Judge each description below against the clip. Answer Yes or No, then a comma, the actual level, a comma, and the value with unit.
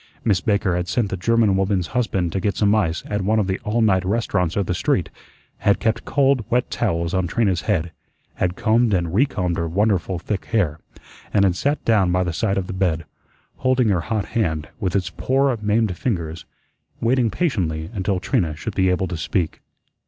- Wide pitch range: No, average, 3.9 semitones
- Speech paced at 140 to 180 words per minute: No, average, 195 wpm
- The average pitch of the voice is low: Yes, very low, 95 Hz